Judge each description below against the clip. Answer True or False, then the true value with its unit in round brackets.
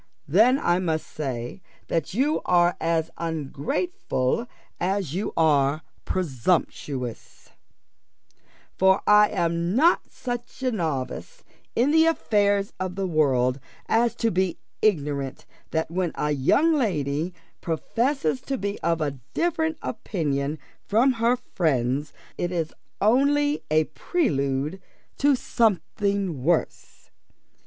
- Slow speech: True (115 wpm)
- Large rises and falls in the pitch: True (7.6 semitones)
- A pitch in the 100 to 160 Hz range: False (180 Hz)